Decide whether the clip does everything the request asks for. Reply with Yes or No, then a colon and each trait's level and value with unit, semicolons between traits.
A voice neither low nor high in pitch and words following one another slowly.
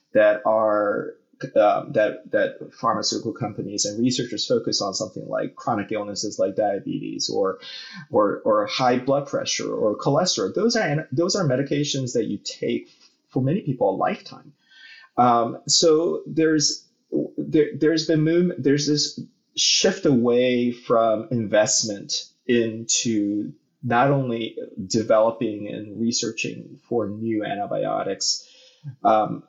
No: low, 125 Hz; slow, 120 wpm